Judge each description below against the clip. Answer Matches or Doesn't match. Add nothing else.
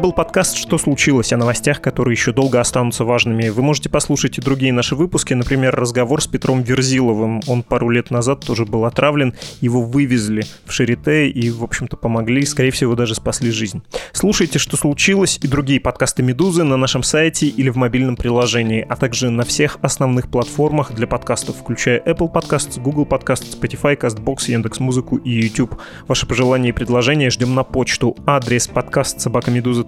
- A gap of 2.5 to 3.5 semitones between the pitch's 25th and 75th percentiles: Matches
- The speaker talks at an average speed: Doesn't match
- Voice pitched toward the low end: Matches